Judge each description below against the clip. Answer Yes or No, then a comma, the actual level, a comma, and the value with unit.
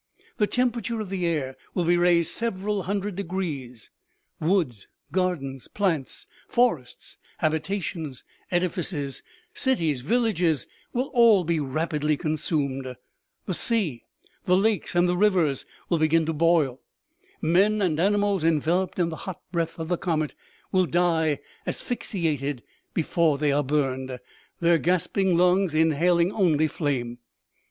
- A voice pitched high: No, medium, 170 Hz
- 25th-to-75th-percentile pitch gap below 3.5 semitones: No, average, 3.9 semitones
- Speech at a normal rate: No, slow, 130 wpm